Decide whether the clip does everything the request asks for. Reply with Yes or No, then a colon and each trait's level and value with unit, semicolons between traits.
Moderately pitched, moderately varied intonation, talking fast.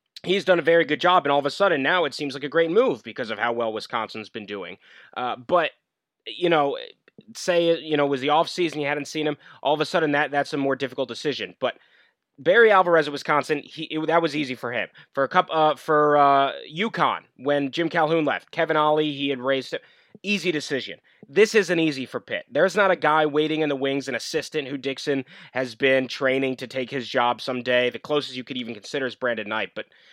Yes: medium, 145 Hz; average, 3.7 semitones; fast, 230 wpm